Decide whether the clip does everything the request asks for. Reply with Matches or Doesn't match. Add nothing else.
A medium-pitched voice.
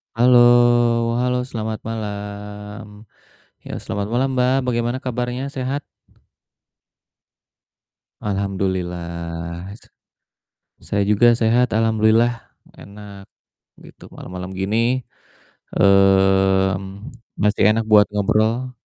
Doesn't match